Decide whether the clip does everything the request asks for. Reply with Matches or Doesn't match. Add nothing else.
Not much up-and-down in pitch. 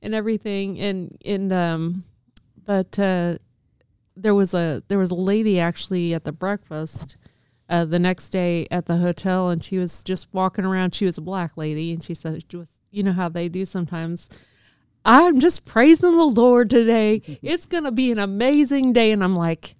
Doesn't match